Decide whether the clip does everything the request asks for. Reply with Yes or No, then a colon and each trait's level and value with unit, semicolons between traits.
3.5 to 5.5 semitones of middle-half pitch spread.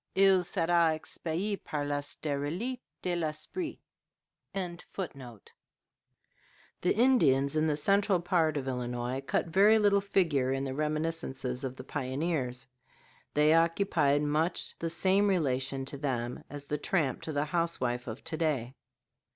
Yes: average, 4.6 semitones